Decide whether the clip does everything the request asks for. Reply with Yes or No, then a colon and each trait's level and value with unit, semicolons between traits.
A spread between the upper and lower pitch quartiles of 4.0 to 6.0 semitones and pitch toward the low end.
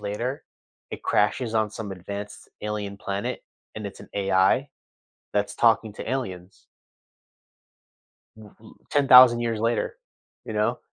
No: average, 2.9 semitones; low, 105 Hz